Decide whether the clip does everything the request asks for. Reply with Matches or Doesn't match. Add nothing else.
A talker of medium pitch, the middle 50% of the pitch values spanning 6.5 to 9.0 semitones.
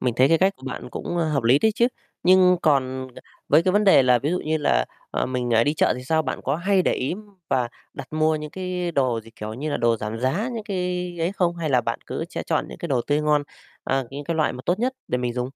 Doesn't match